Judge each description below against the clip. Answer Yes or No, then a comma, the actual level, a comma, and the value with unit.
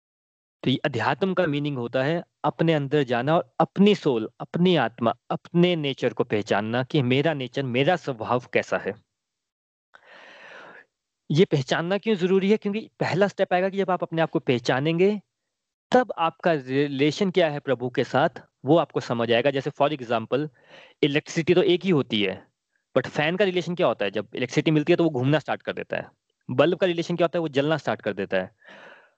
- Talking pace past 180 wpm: Yes, fast, 190 wpm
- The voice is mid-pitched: Yes, medium, 155 Hz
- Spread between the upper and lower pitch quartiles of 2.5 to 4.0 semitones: No, average, 4.9 semitones